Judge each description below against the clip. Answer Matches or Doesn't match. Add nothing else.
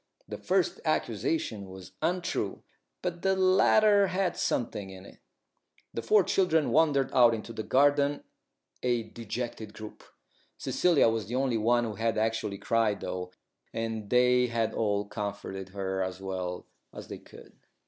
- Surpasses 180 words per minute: Doesn't match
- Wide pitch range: Matches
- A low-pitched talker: Matches